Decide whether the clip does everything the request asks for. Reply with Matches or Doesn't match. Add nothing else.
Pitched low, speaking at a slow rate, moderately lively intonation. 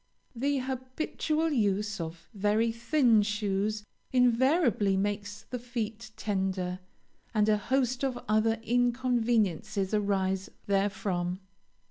Doesn't match